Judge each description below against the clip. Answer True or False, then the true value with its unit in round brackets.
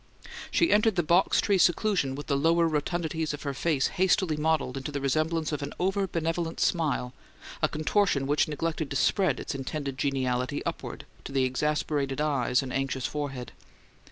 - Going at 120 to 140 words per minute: False (170 wpm)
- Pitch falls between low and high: True (150 Hz)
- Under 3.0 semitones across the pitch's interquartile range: False (3.5 semitones)